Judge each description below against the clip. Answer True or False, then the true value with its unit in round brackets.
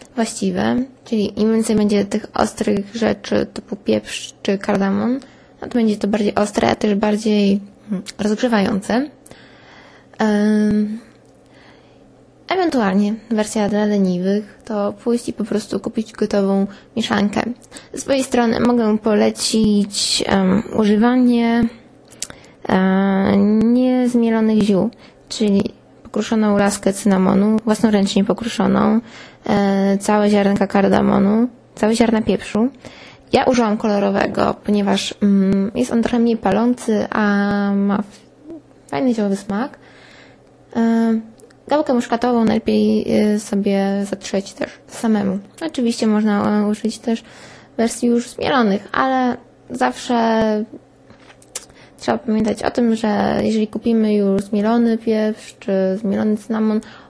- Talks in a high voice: True (215 Hz)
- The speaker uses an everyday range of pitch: False (2.3 semitones)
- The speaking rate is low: True (105 wpm)